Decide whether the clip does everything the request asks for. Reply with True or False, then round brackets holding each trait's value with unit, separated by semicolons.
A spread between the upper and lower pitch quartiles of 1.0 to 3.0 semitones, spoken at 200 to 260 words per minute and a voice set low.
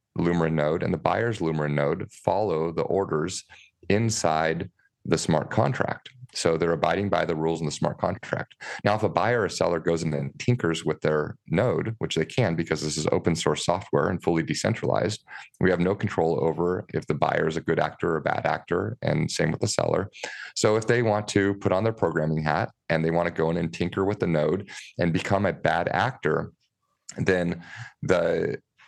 False (3.8 semitones; 205 wpm; 85 Hz)